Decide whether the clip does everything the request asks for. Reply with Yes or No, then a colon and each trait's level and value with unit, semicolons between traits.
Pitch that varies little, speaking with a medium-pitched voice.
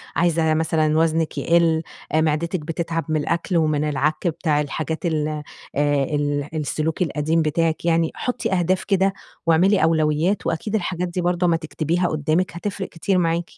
Yes: narrow, 2.1 semitones; medium, 165 Hz